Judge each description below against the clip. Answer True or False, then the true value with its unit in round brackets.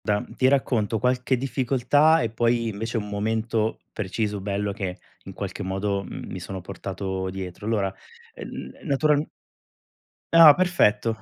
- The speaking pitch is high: False (110 Hz)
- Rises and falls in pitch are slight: False (4.2 semitones)